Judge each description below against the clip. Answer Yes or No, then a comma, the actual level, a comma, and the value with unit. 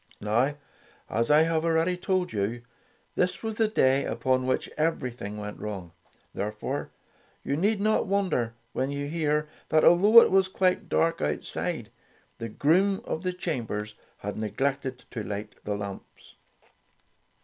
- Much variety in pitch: Yes, wide, 8.6 semitones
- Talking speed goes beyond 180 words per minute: No, average, 150 wpm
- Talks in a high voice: No, medium, 140 Hz